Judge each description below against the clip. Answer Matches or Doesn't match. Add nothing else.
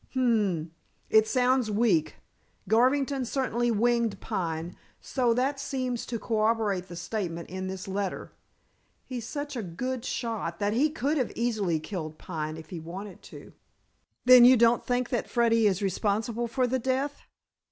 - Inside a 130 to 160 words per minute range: Matches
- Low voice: Doesn't match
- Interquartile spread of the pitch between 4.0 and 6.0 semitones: Matches